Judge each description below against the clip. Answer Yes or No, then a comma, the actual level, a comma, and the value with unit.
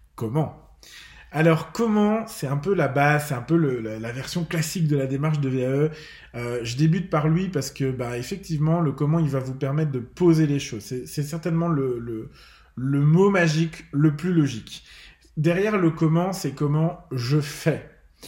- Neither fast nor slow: Yes, average, 190 wpm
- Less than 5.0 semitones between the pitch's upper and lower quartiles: Yes, average, 3.7 semitones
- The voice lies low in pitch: No, medium, 150 Hz